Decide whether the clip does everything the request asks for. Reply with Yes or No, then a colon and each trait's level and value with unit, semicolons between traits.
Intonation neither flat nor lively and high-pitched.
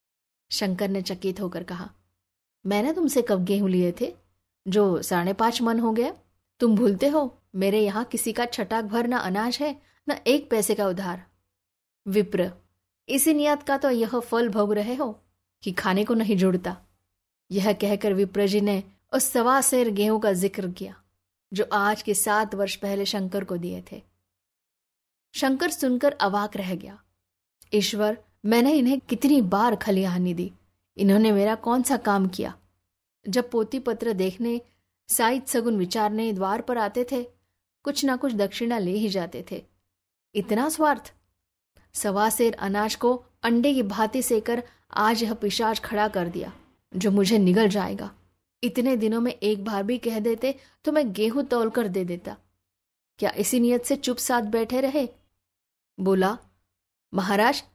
Yes: average, 4.6 semitones; high, 210 Hz